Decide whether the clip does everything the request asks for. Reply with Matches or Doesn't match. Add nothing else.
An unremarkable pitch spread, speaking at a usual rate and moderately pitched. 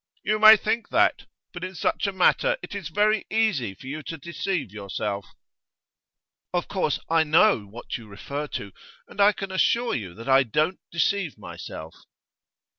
Doesn't match